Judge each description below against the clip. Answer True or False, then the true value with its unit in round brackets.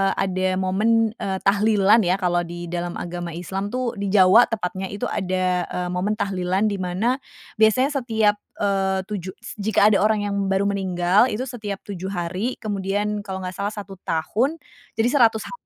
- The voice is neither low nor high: False (195 Hz)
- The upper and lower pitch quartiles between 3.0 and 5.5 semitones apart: False (2.6 semitones)